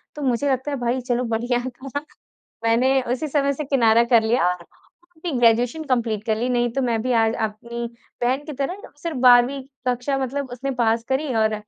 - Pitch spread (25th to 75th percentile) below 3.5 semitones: Yes, average, 2.8 semitones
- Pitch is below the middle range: No, very high, 250 Hz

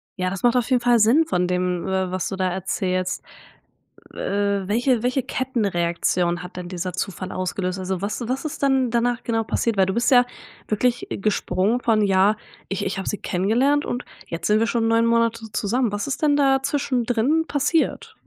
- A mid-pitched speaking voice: No, high, 215 Hz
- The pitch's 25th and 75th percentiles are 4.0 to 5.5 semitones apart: Yes, average, 4.7 semitones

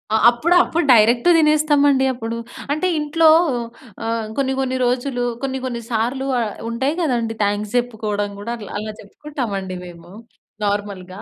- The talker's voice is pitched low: No, high, 235 Hz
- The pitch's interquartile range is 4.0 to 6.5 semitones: Yes, average, 4.5 semitones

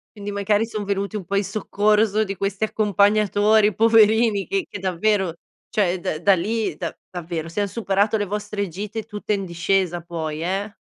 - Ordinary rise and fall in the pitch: No, narrow, 2.2 semitones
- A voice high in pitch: Yes, high, 200 Hz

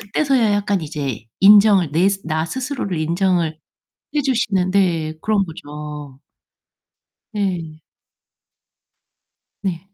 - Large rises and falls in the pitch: No, average, 4.6 semitones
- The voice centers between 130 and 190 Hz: Yes, medium, 185 Hz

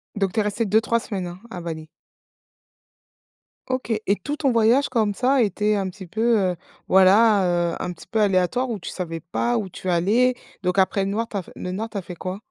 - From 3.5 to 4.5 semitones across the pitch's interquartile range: Yes, average, 3.8 semitones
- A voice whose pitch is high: Yes, high, 200 Hz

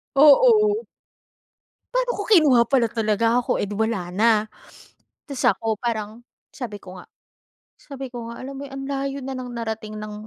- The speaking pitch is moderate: No, high, 240 Hz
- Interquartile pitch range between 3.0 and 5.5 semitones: Yes, average, 4.0 semitones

